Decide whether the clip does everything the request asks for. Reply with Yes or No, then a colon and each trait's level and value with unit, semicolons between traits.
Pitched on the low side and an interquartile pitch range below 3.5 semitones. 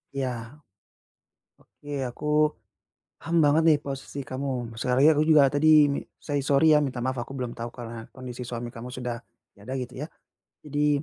Yes: low, 130 Hz; average, 3.0 semitones